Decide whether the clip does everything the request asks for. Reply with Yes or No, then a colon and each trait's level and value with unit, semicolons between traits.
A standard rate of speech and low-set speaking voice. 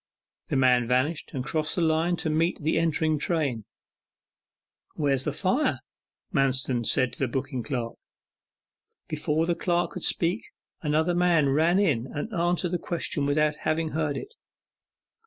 No: average, 155 wpm; medium, 155 Hz